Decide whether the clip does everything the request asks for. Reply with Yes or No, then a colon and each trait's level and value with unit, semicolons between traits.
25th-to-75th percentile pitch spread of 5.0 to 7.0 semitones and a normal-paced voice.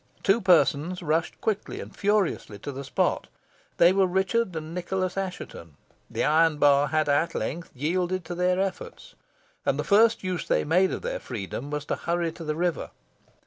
No: average, 3.7 semitones; average, 180 wpm